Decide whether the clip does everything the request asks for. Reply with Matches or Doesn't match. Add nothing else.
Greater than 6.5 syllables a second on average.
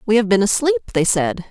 Doesn't match